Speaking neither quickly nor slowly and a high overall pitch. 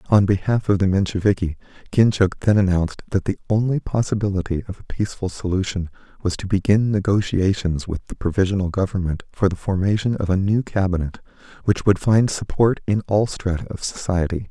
No: average, 165 wpm; very low, 95 Hz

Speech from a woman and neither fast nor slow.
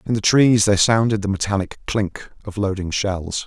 No: male; average, 190 wpm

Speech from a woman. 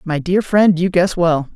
No: male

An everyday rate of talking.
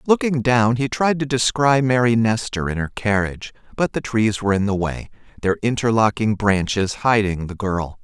Yes: average, 180 wpm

